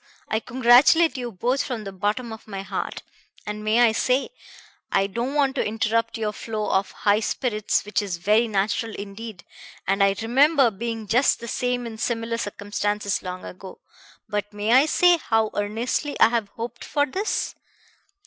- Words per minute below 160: No, average, 170 wpm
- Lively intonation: No, average, 2.9 semitones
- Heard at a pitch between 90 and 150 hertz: No, high, 225 Hz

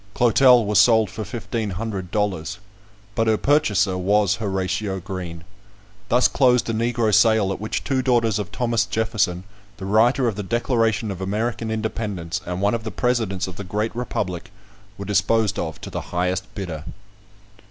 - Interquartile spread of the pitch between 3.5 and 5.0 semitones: No, average, 3.1 semitones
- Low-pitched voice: Yes, low, 105 Hz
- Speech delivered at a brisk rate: No, average, 165 wpm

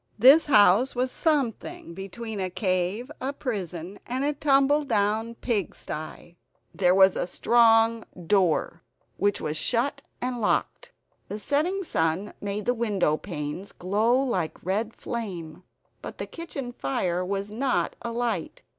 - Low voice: No, high, 215 Hz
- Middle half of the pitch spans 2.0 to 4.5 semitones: No, average, 5.3 semitones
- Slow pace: Yes, slow, 130 wpm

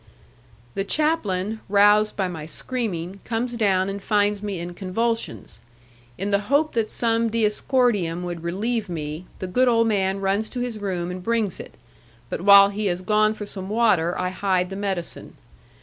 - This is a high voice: Yes, high, 200 Hz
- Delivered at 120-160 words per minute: No, average, 170 wpm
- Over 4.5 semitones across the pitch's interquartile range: No, average, 3.5 semitones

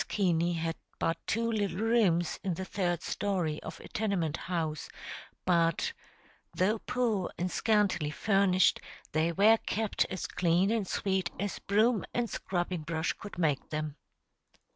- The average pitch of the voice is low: No, medium, 185 Hz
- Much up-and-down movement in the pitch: No, average, 3.7 semitones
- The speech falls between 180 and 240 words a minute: No, average, 140 wpm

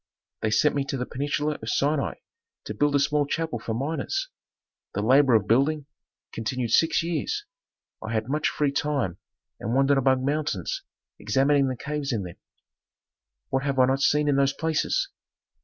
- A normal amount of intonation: Yes, average, 3.3 semitones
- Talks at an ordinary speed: Yes, average, 170 wpm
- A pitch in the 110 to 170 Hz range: Yes, medium, 140 Hz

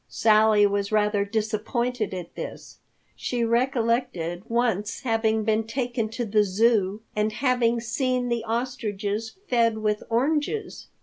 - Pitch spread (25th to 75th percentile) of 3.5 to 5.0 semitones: No, narrow, 2.4 semitones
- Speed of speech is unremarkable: No, slow, 125 wpm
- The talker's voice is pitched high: Yes, high, 225 Hz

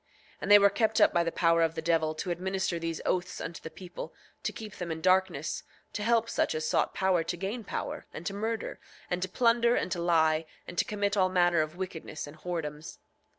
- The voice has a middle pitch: Yes, medium, 175 Hz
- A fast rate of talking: Yes, fast, 230 wpm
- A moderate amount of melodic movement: Yes, average, 3.3 semitones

